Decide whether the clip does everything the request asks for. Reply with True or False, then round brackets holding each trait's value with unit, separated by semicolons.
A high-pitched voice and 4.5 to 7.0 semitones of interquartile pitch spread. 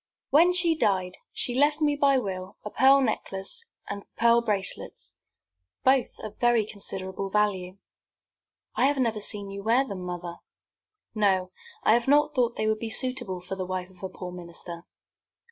True (210 Hz; 5.5 semitones)